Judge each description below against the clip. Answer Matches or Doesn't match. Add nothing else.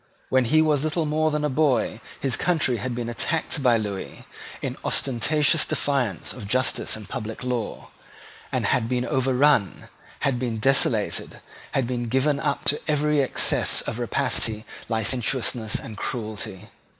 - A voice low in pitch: Matches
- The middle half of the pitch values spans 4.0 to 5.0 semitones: Matches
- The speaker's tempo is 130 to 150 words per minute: Matches